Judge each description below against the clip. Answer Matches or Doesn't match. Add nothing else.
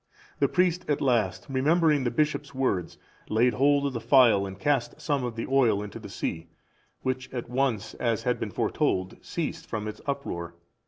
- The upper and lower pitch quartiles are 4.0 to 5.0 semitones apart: Matches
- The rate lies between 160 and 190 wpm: Matches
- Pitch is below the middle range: Matches